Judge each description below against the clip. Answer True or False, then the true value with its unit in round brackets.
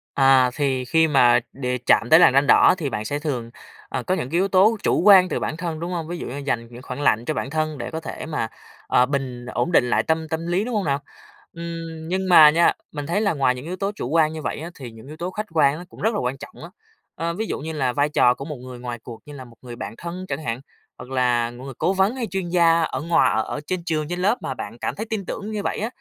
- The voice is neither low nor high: True (155 Hz)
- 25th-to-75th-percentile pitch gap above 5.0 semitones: True (5.4 semitones)